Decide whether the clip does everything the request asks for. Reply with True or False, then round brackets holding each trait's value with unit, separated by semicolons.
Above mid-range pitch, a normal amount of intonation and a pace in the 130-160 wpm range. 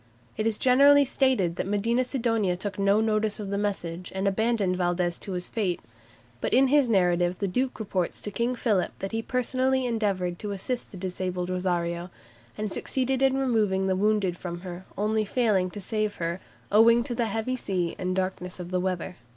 False (200 Hz; 4.2 semitones; 190 wpm)